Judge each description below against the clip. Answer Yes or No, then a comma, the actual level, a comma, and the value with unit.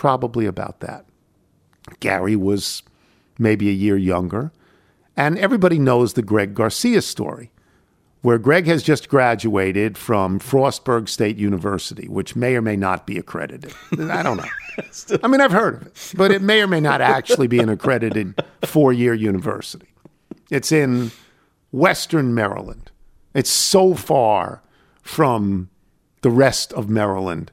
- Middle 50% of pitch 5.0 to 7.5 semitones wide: Yes, wide, 5.6 semitones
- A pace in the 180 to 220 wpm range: No, average, 145 wpm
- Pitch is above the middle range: No, low, 115 Hz